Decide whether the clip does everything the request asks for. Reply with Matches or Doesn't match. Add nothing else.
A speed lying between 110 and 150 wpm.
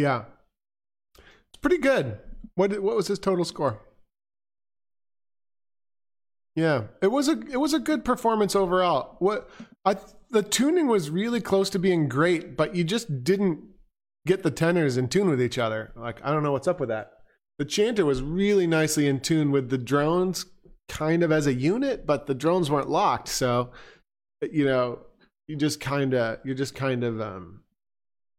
Doesn't match